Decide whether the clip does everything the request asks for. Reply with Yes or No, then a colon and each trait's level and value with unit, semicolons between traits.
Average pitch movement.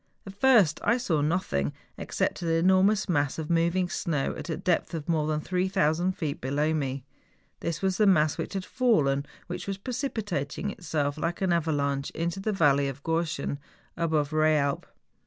Yes: average, 4.2 semitones